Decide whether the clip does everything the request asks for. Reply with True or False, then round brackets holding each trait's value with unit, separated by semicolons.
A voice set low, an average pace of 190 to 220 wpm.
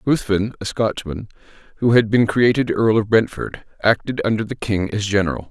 False (110 Hz; 175 wpm)